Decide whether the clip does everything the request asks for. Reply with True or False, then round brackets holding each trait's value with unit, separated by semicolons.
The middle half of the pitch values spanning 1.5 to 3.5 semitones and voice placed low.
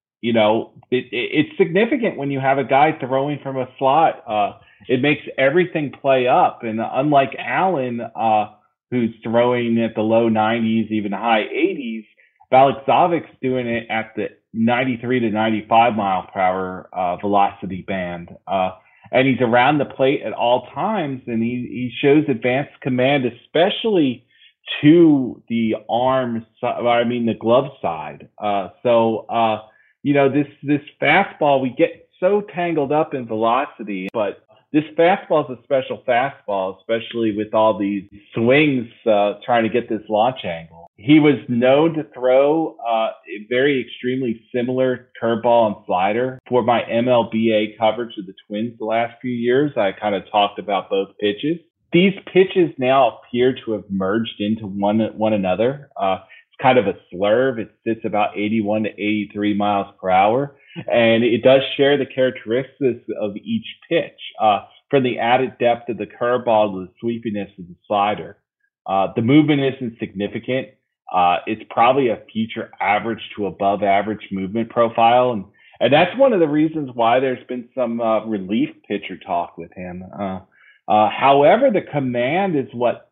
False (4.0 semitones; 120 Hz)